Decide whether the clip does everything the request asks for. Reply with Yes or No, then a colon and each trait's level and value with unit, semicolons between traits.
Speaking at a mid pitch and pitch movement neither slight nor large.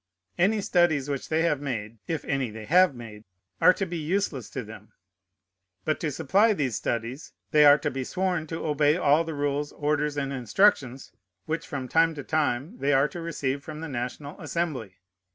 Yes: medium, 145 Hz; average, 3.8 semitones